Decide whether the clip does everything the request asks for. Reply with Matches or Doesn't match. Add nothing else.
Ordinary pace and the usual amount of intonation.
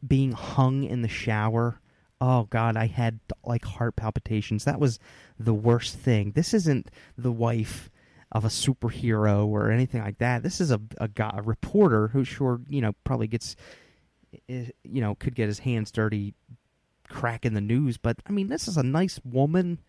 Matches